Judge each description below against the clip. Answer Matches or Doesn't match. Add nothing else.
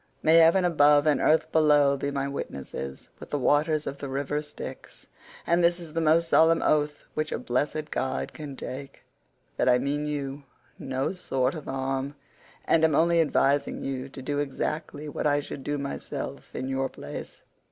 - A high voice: Doesn't match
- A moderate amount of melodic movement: Doesn't match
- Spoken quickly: Doesn't match